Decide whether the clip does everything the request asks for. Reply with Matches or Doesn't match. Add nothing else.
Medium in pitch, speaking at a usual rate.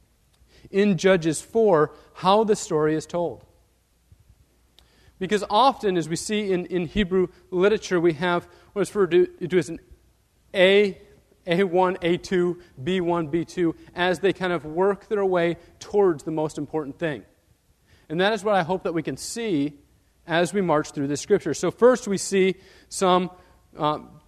Matches